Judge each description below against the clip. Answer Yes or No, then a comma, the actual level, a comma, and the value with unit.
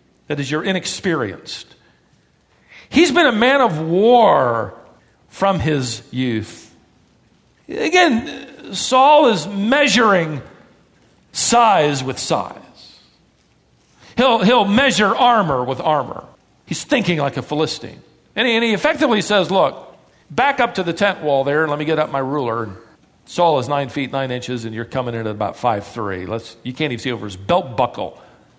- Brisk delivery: No, average, 155 wpm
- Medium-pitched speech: Yes, medium, 155 Hz